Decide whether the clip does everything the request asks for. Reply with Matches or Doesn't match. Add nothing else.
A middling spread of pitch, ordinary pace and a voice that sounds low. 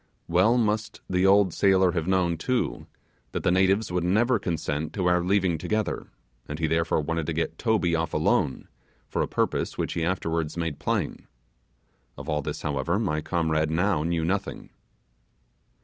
Matches